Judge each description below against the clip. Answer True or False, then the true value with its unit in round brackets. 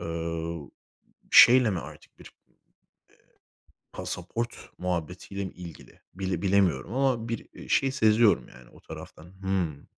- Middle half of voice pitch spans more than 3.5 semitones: True (5.2 semitones)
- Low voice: True (95 Hz)